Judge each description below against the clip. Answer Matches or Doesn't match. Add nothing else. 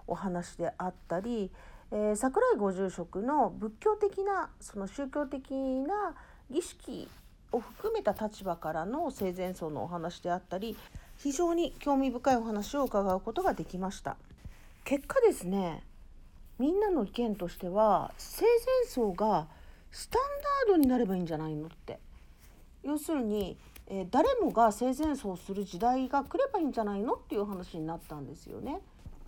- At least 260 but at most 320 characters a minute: Matches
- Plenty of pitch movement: Matches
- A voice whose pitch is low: Doesn't match